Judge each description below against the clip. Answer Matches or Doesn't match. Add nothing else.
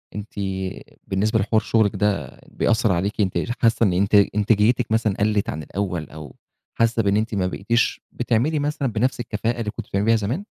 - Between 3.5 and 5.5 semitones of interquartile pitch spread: Doesn't match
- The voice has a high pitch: Doesn't match